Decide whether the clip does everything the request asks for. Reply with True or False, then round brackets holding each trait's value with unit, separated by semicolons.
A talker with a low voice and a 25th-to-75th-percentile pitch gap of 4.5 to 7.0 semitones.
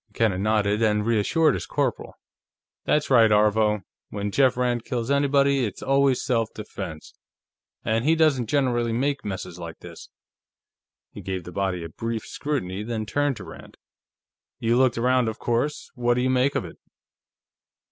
False (115 Hz; 4.1 semitones)